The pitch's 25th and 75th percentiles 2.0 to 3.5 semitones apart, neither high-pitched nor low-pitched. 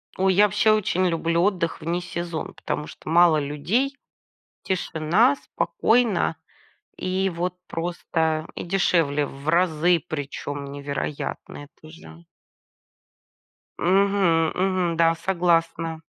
Yes: average, 3.0 semitones; medium, 170 Hz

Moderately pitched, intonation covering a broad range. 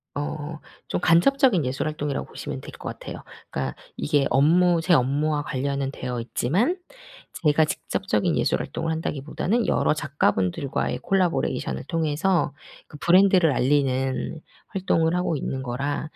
No: medium, 150 Hz; average, 4.0 semitones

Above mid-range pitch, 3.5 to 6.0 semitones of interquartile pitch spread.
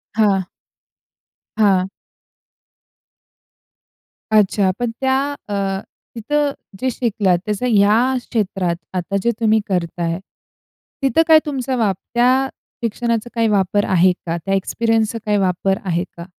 Yes: high, 210 Hz; average, 3.9 semitones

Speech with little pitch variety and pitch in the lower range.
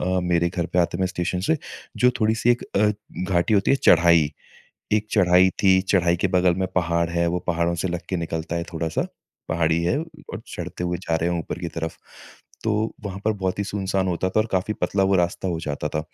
Yes: narrow, 2.3 semitones; very low, 90 Hz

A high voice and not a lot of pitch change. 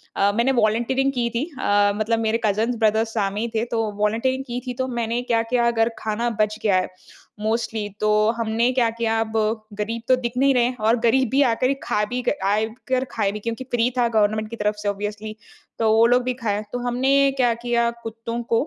Yes: high, 230 Hz; narrow, 2.1 semitones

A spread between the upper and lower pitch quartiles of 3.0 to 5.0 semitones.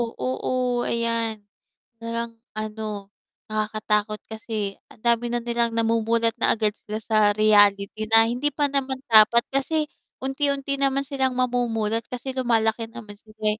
No: narrow, 2.6 semitones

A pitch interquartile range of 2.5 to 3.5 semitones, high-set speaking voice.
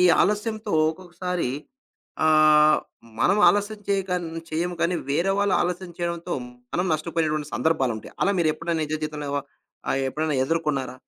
No: average, 2.9 semitones; medium, 165 Hz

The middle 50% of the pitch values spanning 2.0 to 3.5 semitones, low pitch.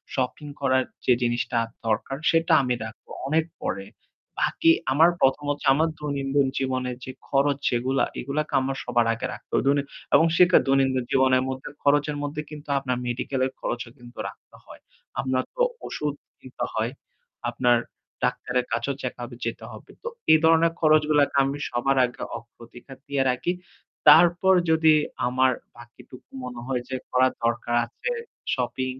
Yes: average, 2.8 semitones; low, 130 Hz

